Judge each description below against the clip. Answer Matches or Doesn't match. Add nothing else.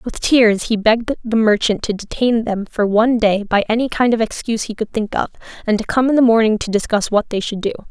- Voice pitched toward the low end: Doesn't match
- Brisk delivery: Matches